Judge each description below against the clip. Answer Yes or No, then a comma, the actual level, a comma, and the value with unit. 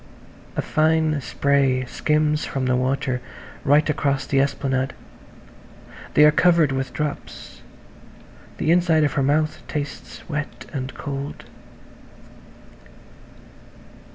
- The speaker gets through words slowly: Yes, slow, 105 wpm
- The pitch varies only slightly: Yes, narrow, 2.3 semitones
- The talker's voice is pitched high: No, medium, 145 Hz